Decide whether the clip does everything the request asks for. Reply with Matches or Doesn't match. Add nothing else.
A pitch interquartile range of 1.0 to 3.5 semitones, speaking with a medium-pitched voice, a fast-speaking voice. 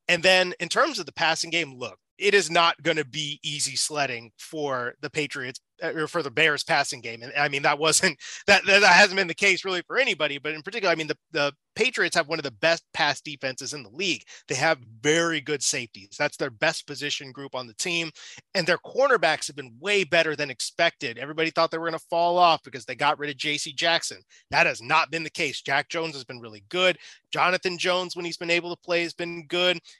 Matches